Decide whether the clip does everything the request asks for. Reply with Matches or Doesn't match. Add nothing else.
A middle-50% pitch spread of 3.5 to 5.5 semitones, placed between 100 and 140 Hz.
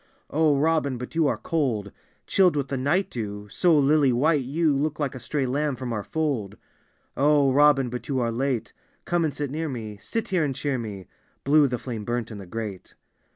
Matches